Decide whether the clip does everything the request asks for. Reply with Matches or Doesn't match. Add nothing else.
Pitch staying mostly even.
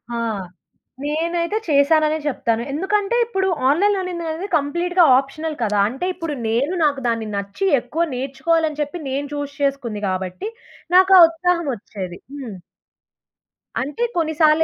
Doesn't match